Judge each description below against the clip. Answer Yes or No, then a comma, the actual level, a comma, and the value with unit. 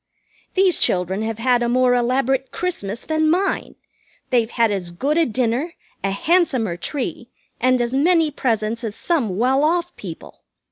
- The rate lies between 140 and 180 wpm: Yes, average, 155 wpm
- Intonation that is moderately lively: No, wide, 5.9 semitones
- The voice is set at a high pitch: Yes, very high, 250 Hz